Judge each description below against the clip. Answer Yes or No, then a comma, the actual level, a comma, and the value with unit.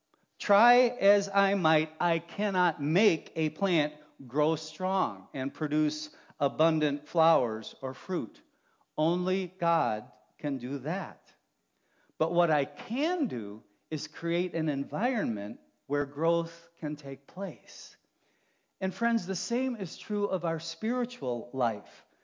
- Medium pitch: Yes, medium, 165 Hz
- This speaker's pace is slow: Yes, slow, 125 wpm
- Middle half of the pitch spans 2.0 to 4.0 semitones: No, average, 4.7 semitones